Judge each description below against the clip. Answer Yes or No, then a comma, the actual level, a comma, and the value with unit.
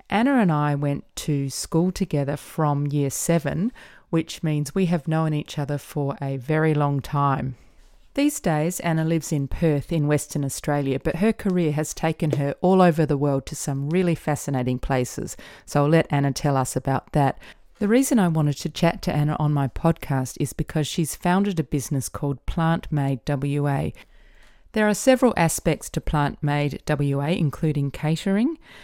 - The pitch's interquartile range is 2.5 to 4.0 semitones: Yes, average, 3.0 semitones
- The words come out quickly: No, average, 175 wpm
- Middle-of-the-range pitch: Yes, medium, 150 Hz